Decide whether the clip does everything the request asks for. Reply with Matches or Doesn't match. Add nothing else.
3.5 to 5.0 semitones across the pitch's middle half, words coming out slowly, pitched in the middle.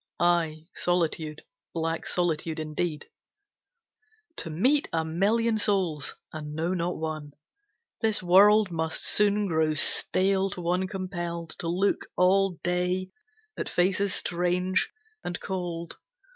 Doesn't match